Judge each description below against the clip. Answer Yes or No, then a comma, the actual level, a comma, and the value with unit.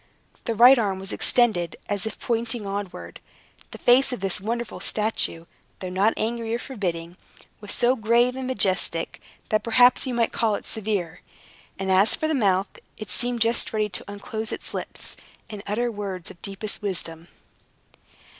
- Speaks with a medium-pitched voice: No, high, 215 Hz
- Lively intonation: No, average, 3.6 semitones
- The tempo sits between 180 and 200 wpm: No, average, 170 wpm